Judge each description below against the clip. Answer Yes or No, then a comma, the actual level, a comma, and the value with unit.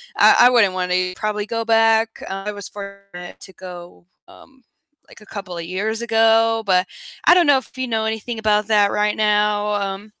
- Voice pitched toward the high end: Yes, high, 210 Hz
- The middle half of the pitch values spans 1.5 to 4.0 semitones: Yes, narrow, 2.5 semitones